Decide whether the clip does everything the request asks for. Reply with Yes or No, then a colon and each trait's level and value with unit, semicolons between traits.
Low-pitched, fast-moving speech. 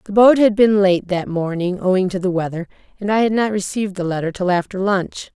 No: high, 190 Hz; fast, 235 wpm